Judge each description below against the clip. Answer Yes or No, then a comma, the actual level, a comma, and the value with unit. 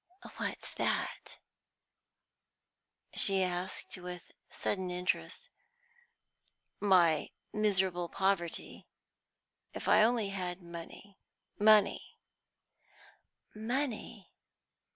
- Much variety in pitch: No, average, 2.8 semitones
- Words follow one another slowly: Yes, slow, 70 wpm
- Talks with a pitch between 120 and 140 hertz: No, high, 190 Hz